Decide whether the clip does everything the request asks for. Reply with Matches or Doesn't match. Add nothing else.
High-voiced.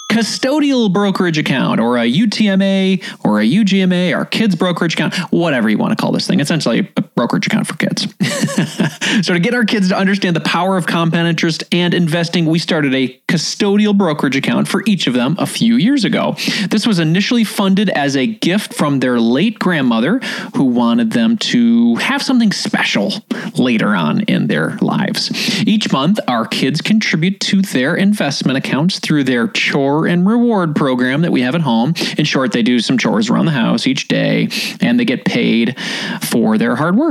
Matches